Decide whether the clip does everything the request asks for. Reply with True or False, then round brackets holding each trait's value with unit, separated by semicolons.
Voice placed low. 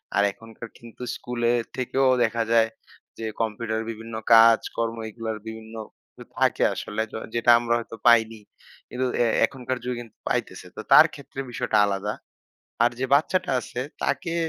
True (115 Hz)